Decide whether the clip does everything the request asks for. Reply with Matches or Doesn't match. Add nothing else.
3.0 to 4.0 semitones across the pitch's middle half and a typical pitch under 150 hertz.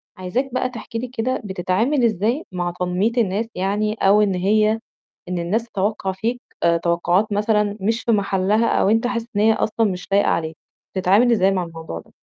Doesn't match